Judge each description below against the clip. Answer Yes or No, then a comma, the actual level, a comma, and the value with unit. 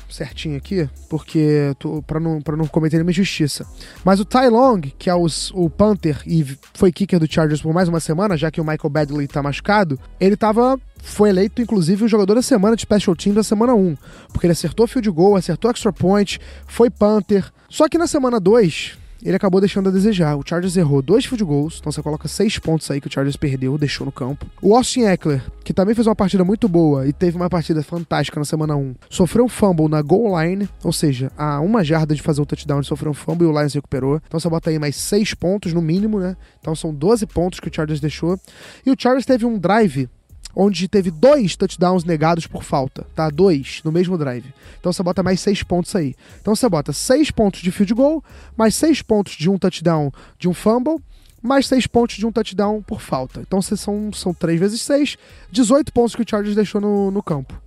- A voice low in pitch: No, medium, 180 Hz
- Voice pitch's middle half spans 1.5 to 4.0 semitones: No, wide, 5.4 semitones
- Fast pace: Yes, fast, 225 wpm